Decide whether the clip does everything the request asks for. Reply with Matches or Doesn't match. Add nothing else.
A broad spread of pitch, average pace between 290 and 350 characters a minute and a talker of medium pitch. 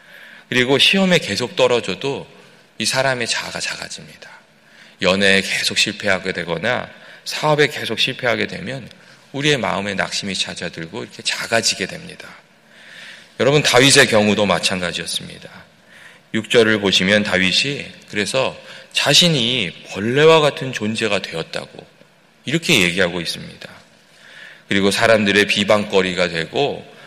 Doesn't match